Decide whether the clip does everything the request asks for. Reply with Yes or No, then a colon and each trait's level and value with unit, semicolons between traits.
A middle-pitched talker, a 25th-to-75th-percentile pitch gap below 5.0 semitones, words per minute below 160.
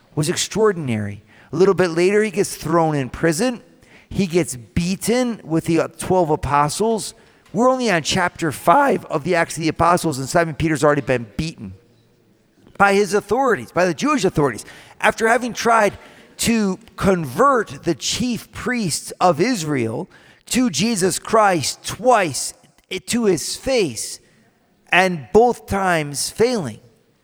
No: medium, 180 Hz; wide, 5.5 semitones; average, 140 wpm